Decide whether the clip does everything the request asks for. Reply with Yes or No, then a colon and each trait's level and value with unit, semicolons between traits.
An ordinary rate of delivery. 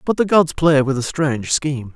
No: fast, 245 wpm